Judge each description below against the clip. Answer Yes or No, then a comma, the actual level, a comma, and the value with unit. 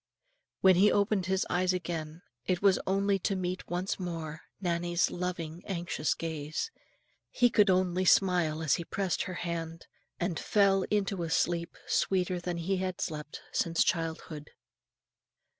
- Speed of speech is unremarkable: Yes, average, 145 wpm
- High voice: No, medium, 180 Hz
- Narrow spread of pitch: Yes, narrow, 2.3 semitones